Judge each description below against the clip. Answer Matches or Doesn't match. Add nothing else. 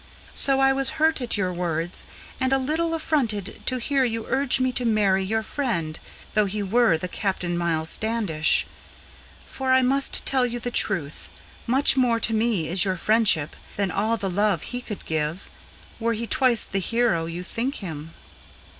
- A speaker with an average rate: Matches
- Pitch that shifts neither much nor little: Doesn't match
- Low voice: Doesn't match